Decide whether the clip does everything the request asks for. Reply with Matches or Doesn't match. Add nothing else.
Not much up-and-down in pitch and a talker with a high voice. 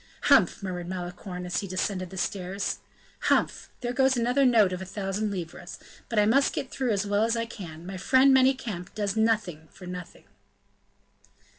Doesn't match